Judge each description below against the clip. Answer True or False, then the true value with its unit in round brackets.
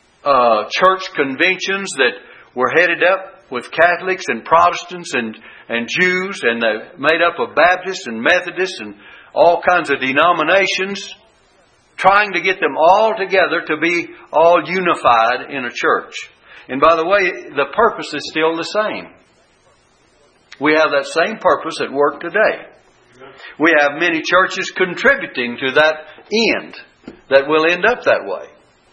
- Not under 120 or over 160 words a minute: True (145 wpm)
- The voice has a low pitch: False (175 Hz)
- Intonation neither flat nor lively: True (3.6 semitones)